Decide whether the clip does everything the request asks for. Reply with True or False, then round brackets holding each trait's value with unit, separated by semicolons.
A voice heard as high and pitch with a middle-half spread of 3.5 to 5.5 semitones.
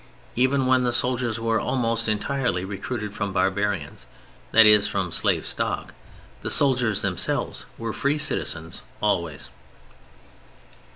False (110 Hz; 4.0 semitones)